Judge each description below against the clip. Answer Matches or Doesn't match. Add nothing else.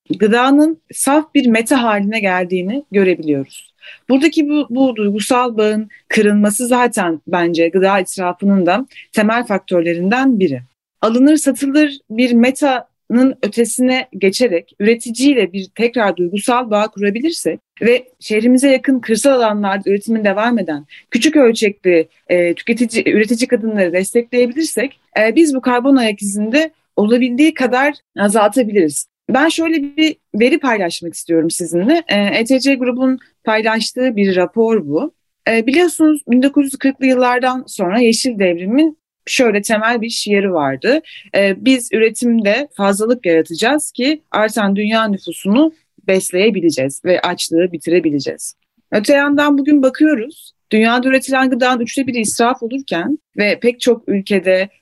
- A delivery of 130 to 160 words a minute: Doesn't match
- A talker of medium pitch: Doesn't match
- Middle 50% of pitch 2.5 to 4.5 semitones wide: Doesn't match